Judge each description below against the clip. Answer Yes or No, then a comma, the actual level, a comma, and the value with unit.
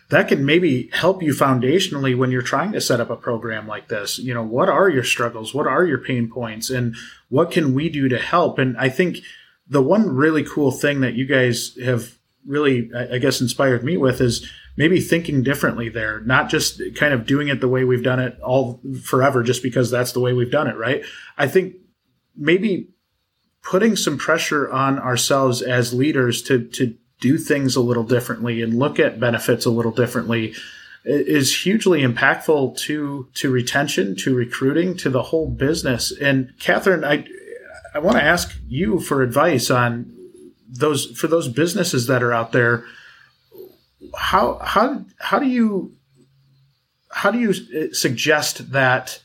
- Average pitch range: Yes, average, 3.3 semitones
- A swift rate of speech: No, average, 175 wpm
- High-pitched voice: No, low, 130 Hz